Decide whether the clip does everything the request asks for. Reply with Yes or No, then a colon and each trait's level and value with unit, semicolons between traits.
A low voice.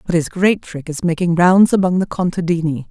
No: medium, 170 Hz